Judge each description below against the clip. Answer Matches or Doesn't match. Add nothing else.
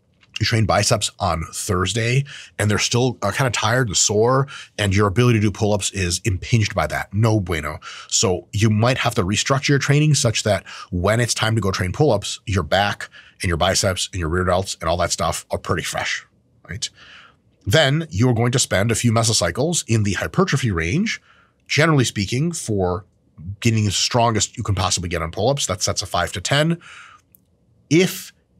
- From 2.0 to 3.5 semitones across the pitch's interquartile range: Doesn't match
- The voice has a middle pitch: Doesn't match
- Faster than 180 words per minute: Matches